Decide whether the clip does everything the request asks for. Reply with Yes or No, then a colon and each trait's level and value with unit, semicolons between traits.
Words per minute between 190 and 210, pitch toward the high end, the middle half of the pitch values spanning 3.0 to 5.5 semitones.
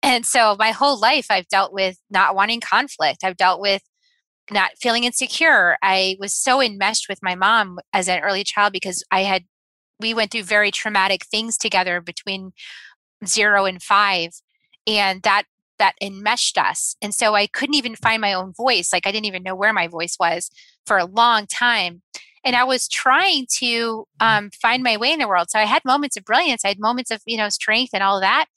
Yes: fast, 205 wpm; high, 210 Hz; average, 3.4 semitones